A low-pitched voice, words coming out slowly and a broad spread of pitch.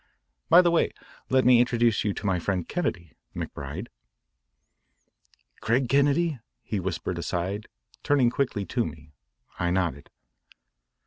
Yes: low, 105 Hz; slow, 125 wpm; wide, 6.9 semitones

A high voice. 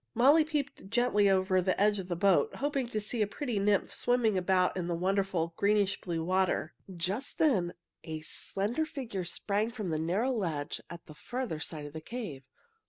Yes: high, 195 Hz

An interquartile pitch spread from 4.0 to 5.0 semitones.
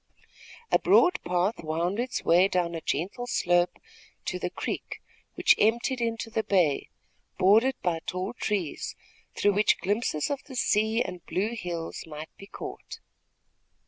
Yes: average, 4.6 semitones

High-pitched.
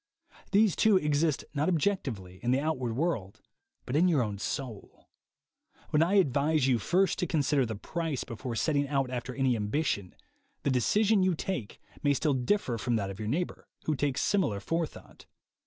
No: medium, 140 Hz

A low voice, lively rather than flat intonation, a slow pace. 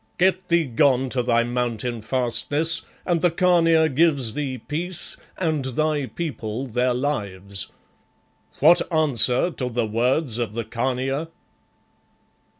No: low, 130 Hz; average, 5.0 semitones; slow, 125 wpm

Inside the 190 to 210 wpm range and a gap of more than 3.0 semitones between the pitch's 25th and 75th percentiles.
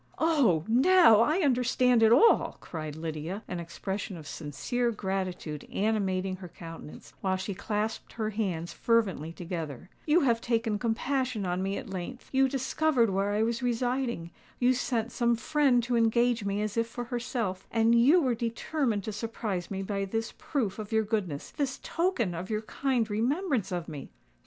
No: average, 160 wpm; average, 4.6 semitones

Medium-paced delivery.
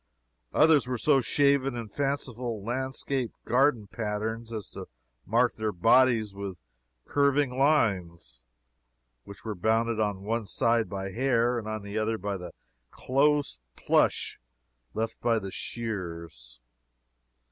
No: slow, 125 wpm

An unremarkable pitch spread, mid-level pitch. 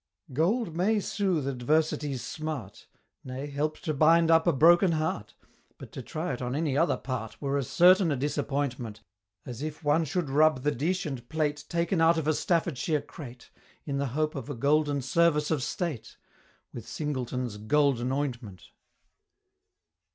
Yes: average, 3.6 semitones; medium, 150 Hz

